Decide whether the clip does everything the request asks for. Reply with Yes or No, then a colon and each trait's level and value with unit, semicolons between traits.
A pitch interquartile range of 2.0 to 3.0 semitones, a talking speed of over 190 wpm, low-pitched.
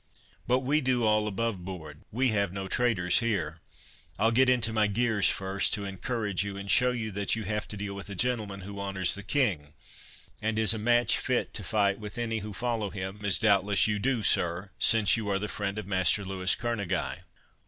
Yes: average, 2.7 semitones; fast, 205 wpm; low, 105 Hz